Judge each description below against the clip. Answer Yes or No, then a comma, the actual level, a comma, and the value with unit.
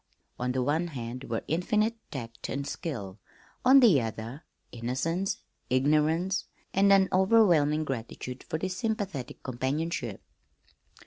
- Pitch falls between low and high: Yes, medium, 150 Hz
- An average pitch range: No, wide, 6.8 semitones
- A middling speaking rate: No, slow, 120 wpm